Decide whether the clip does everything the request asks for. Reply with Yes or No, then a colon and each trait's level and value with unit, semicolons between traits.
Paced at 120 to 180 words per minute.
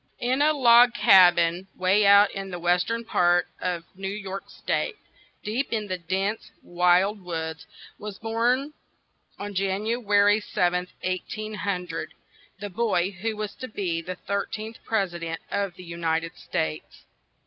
Yes: average, 165 wpm